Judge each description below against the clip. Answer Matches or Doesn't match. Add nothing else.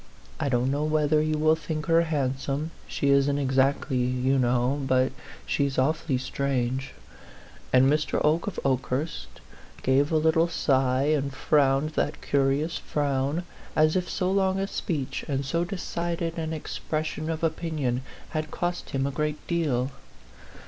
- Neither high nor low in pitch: Matches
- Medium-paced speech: Matches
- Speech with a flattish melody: Doesn't match